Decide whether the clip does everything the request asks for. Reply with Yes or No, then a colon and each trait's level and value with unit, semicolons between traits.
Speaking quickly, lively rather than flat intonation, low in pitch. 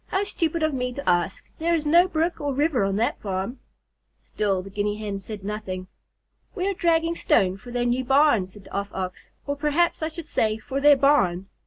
No: fast, 210 wpm; wide, 7.9 semitones; very high, 250 Hz